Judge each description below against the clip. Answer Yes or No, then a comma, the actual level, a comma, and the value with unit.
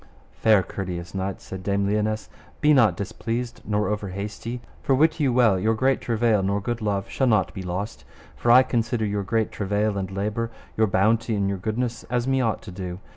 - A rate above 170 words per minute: Yes, average, 200 wpm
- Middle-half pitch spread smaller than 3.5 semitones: Yes, average, 3.0 semitones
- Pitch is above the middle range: No, low, 105 Hz